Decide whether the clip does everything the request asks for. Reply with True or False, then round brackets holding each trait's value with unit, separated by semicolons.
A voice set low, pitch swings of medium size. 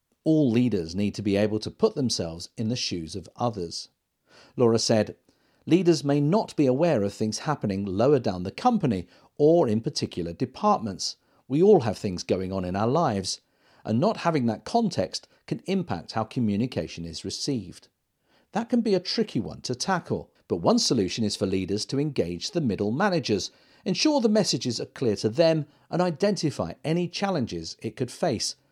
False (120 Hz; 8.7 semitones)